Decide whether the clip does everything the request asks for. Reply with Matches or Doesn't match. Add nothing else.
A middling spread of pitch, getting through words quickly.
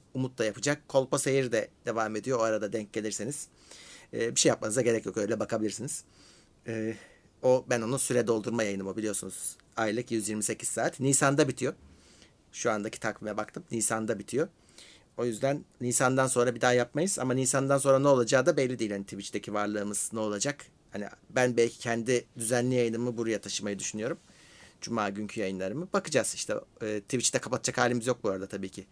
Matches